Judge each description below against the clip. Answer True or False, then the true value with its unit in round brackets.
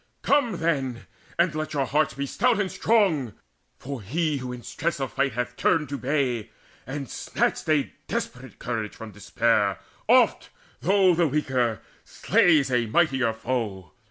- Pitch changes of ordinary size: True (4.7 semitones)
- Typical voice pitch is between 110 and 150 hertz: True (135 Hz)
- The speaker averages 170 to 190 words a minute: False (155 wpm)